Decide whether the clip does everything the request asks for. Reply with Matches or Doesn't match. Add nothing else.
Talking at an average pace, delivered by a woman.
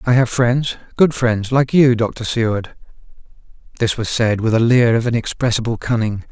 Doesn't match